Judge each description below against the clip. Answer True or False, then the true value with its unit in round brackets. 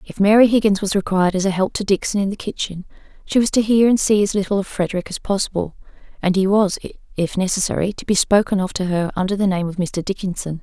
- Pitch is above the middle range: True (195 Hz)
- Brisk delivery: True (235 wpm)